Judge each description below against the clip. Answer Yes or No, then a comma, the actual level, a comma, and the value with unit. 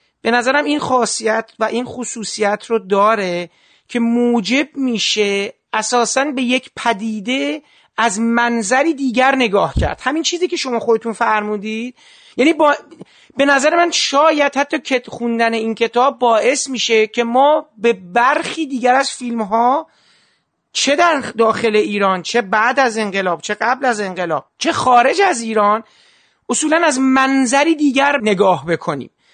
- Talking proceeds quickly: No, average, 145 wpm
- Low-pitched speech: No, high, 240 Hz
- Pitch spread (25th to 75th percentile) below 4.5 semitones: Yes, average, 4.0 semitones